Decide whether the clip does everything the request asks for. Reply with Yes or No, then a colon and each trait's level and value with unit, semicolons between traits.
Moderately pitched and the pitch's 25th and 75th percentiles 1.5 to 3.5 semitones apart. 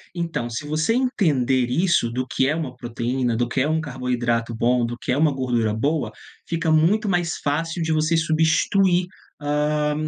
No: medium, 150 Hz; average, 4.8 semitones